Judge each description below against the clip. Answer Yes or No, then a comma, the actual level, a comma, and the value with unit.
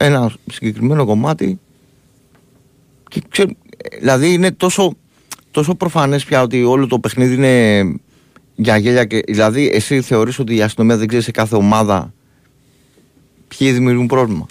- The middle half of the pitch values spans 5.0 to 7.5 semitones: No, average, 4.0 semitones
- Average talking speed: Yes, average, 135 wpm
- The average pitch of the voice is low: Yes, low, 130 Hz